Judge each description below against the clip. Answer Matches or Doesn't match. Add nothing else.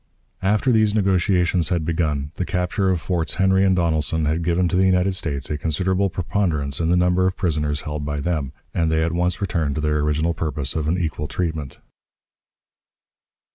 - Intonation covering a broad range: Doesn't match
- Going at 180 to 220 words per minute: Matches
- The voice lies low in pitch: Matches